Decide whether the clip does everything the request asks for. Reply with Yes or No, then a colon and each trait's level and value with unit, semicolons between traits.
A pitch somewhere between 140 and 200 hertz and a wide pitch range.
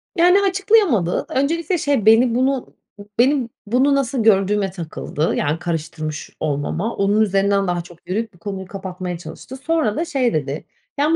No: high, 210 Hz; wide, 7.5 semitones